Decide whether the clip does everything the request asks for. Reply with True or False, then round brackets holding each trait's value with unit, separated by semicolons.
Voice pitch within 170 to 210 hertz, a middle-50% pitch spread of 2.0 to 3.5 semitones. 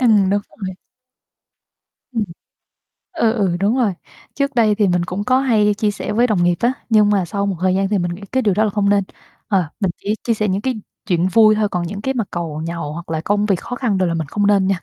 True (205 Hz; 3.0 semitones)